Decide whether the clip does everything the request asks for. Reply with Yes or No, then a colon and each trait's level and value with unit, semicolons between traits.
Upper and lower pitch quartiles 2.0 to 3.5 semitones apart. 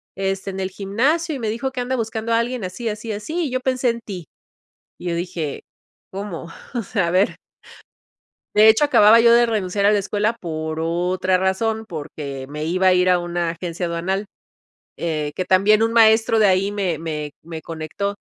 No: average, 4.5 semitones